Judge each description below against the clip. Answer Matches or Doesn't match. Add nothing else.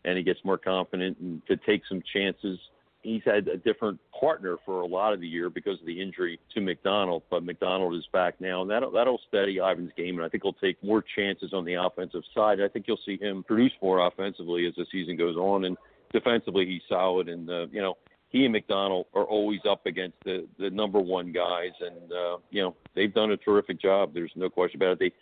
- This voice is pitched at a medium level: Doesn't match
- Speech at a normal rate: Doesn't match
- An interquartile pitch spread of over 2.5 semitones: Doesn't match